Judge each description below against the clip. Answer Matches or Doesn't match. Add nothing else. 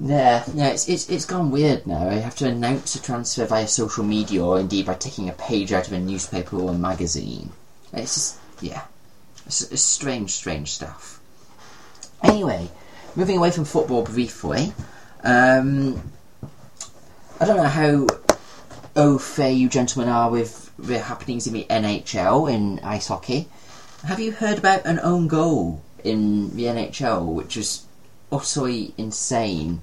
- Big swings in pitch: Matches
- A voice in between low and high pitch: Doesn't match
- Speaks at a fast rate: Doesn't match